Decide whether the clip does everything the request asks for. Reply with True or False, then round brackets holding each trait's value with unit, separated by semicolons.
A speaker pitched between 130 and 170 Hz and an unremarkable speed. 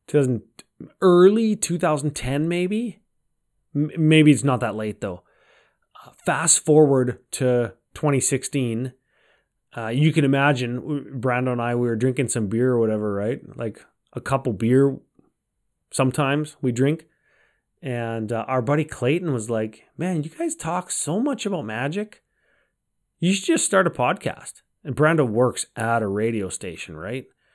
True (135 Hz; 145 wpm)